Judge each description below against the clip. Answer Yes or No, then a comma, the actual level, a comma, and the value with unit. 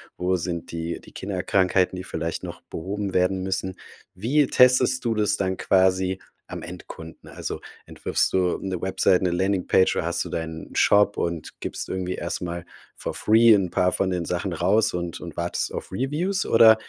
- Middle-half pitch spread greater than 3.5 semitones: No, narrow, 2.6 semitones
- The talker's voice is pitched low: Yes, very low, 95 Hz